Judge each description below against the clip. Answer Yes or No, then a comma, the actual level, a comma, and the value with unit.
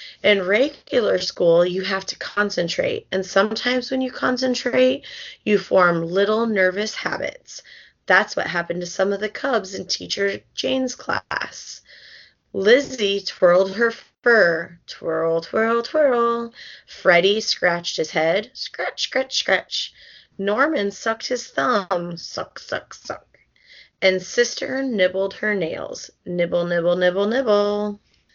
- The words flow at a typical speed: No, slow, 125 wpm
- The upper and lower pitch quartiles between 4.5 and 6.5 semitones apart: Yes, average, 4.8 semitones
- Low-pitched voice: No, high, 205 Hz